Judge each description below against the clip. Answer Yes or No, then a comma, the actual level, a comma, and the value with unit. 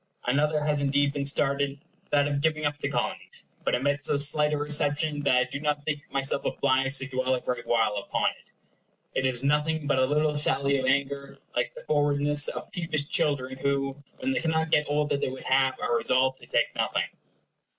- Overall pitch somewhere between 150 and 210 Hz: No, medium, 140 Hz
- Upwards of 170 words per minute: Yes, fast, 205 wpm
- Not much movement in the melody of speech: Yes, narrow, 1.8 semitones